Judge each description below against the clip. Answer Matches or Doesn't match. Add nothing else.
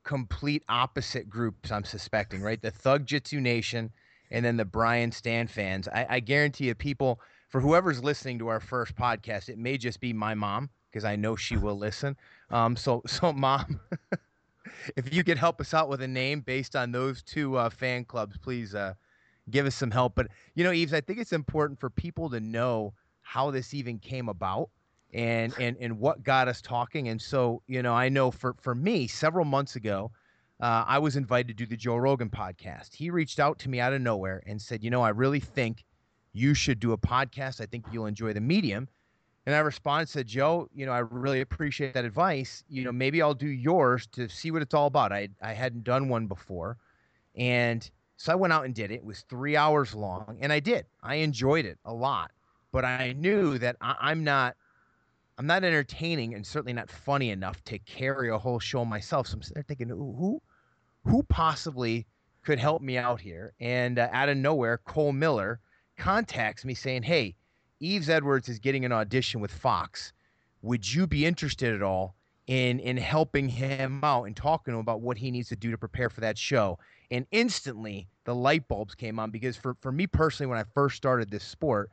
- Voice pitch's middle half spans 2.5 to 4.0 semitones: Matches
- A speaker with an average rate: Doesn't match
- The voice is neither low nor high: Doesn't match